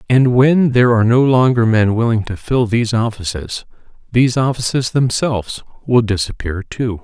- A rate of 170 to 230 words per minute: No, average, 155 wpm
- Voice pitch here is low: Yes, low, 115 Hz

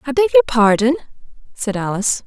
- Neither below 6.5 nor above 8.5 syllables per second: Yes, 7.1 syllables/s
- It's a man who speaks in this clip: No, female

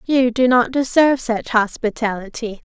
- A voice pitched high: Yes, high, 240 Hz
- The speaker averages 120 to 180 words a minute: Yes, slow, 135 wpm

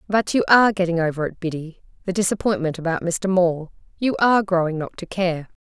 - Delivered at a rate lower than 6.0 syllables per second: No, 6.1 syllables/s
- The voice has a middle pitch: Yes, medium, 180 Hz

